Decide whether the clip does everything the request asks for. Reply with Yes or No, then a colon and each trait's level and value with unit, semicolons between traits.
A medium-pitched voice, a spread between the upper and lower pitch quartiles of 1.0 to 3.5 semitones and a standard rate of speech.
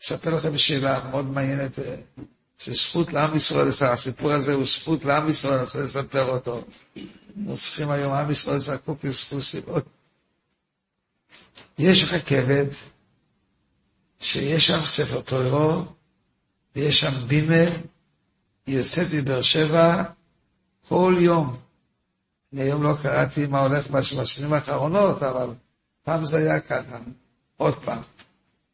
Yes: medium, 145 Hz; average, 2.8 semitones; average, 115 wpm